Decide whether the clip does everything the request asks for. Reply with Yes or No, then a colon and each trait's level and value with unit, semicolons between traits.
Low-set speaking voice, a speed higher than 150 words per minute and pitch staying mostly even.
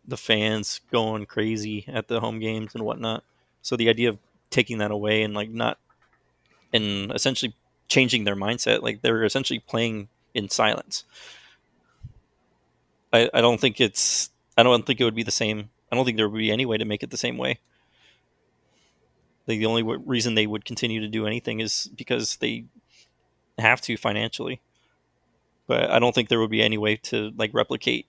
Yes: low, 110 Hz; average, 185 wpm; narrow, 1.8 semitones